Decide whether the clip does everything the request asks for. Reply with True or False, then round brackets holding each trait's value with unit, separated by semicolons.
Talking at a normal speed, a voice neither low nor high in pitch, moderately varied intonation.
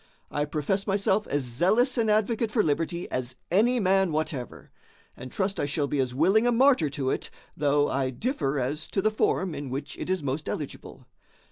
False (195 wpm; 160 Hz; 6.7 semitones)